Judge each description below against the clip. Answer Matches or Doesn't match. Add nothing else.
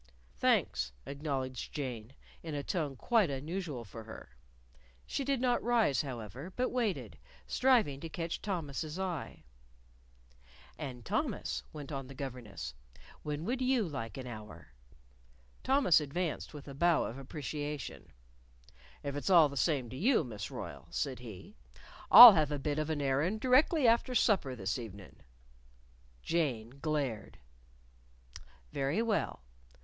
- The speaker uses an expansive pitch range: Matches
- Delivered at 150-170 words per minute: Doesn't match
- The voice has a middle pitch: Matches